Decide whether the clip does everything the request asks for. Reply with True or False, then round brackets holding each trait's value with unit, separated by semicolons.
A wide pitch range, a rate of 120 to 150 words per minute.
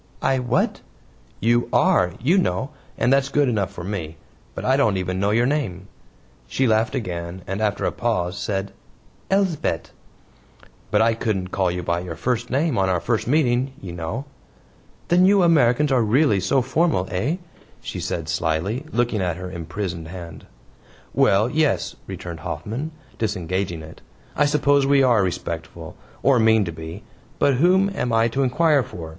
False (7.0 semitones; 170 wpm)